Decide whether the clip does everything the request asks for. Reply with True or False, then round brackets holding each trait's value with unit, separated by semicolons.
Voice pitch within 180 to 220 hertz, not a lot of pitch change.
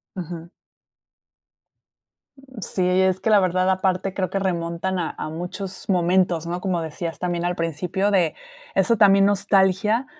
True (185 Hz; 2.0 semitones)